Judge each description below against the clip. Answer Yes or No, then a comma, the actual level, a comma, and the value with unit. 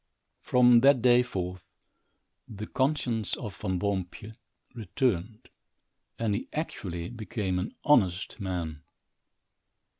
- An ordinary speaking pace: No, slow, 100 wpm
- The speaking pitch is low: Yes, low, 105 Hz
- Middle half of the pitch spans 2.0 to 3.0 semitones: No, average, 4.8 semitones